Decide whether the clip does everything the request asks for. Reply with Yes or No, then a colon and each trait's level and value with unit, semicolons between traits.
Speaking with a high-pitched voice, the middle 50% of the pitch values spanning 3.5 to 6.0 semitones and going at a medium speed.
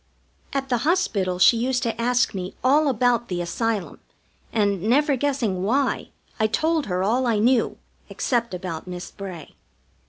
Yes: high, 230 Hz; wide, 5.4 semitones; average, 155 wpm